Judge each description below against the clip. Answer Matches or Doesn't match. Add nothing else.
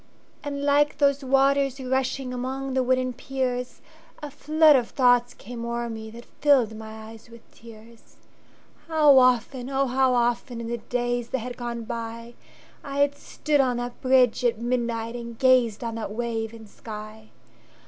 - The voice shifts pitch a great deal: Doesn't match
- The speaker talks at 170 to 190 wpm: Doesn't match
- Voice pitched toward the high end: Matches